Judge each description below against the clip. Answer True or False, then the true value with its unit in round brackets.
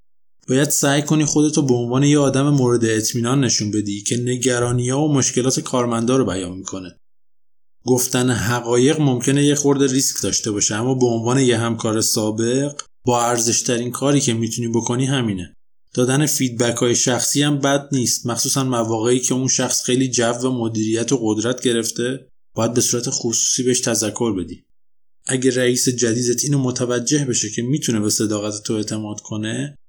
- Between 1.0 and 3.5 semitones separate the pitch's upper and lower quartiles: True (2.4 semitones)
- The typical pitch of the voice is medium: False (125 Hz)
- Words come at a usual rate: False (165 wpm)